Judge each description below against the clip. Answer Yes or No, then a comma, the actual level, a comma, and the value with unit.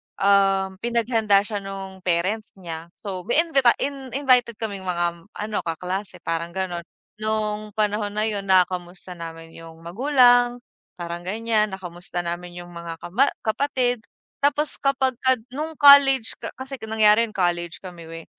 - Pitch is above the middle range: Yes, high, 200 Hz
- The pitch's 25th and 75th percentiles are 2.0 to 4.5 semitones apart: No, average, 5.3 semitones